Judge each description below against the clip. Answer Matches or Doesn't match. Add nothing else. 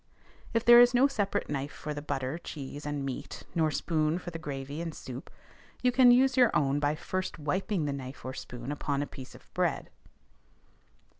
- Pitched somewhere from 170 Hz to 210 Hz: Doesn't match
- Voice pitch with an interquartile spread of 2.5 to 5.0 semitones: Doesn't match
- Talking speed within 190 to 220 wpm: Matches